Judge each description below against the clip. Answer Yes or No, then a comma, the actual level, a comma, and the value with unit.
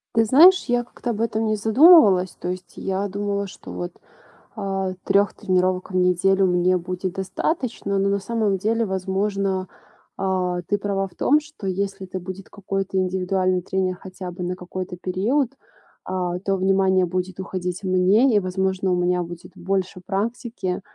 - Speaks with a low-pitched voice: No, high, 190 Hz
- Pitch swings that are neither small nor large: No, narrow, 1.8 semitones